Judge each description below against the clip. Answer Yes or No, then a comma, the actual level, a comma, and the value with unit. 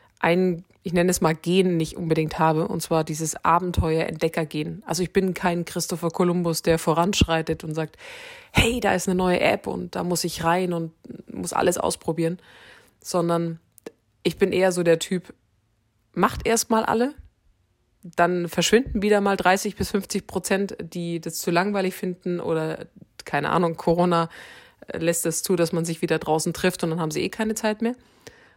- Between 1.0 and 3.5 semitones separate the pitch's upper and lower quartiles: Yes, narrow, 2.4 semitones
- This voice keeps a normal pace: Yes, average, 175 wpm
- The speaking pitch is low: No, medium, 175 Hz